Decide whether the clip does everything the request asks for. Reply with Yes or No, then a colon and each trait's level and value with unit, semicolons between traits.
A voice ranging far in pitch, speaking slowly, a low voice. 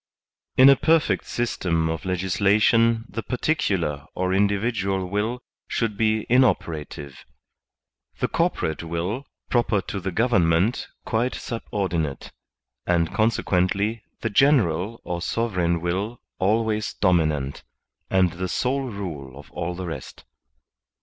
No: average, 5.0 semitones; slow, 120 wpm; very low, 95 Hz